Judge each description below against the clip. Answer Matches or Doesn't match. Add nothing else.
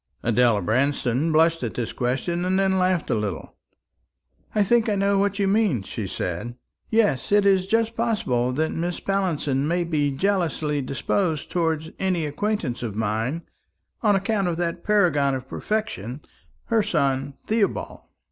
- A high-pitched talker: Doesn't match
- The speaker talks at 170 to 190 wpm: Doesn't match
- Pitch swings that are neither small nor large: Doesn't match